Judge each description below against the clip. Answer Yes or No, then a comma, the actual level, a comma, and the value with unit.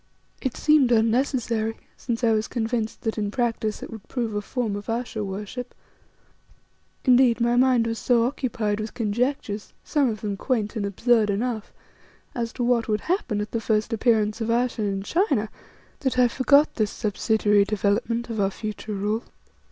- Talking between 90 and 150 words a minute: No, average, 170 wpm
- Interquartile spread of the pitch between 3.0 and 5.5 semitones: No, narrow, 2.6 semitones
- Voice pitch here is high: Yes, high, 225 Hz